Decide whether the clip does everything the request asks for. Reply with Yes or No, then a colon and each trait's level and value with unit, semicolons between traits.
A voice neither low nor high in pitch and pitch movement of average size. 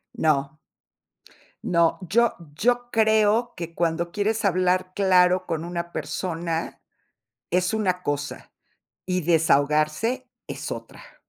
Yes: medium, 180 Hz; average, 4.1 semitones